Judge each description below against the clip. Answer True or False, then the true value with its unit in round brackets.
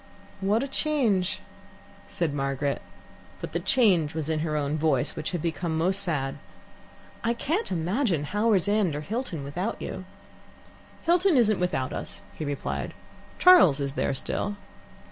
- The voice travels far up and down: True (6.7 semitones)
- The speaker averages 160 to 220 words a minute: False (150 wpm)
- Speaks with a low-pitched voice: False (180 Hz)